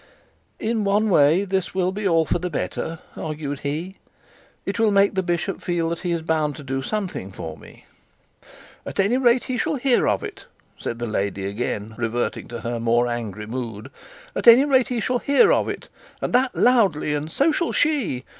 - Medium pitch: Yes, medium, 170 Hz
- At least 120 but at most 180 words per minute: No, average, 190 wpm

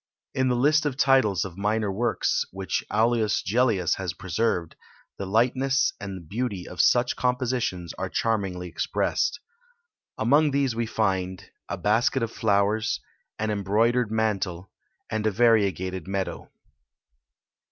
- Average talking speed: No, slow, 130 wpm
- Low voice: Yes, low, 110 Hz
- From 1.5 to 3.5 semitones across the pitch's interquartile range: No, average, 4.1 semitones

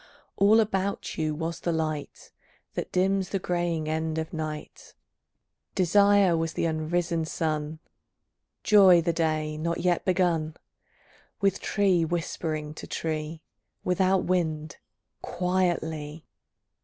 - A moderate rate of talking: No, slow, 115 wpm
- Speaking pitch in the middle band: Yes, medium, 165 Hz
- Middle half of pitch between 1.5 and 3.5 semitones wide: Yes, average, 2.7 semitones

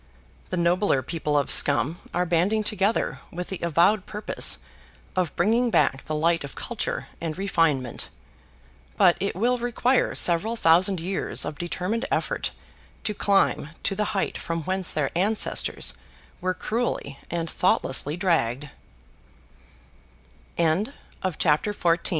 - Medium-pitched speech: Yes, medium, 180 Hz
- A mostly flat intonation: No, average, 4.0 semitones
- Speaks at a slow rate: Yes, slow, 115 wpm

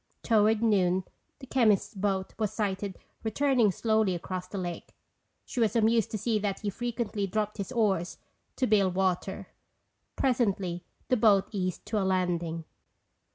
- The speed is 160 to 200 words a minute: No, average, 150 wpm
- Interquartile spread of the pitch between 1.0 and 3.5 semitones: Yes, average, 2.9 semitones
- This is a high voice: Yes, high, 205 Hz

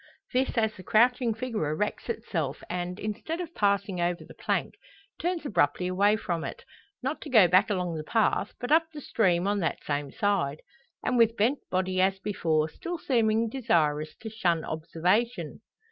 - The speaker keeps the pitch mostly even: No, average, 5.1 semitones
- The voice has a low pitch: No, high, 205 Hz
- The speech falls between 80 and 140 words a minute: No, average, 175 wpm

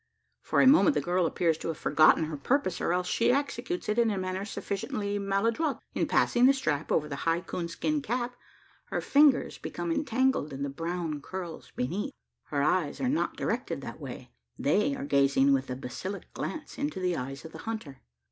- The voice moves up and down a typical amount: No, wide, 8.6 semitones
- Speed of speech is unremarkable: Yes, average, 195 wpm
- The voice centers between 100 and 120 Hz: No, medium, 185 Hz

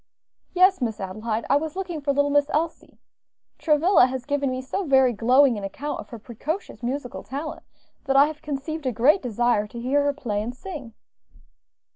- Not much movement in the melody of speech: No, average, 3.8 semitones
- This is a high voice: Yes, very high, 275 Hz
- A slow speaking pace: No, average, 185 wpm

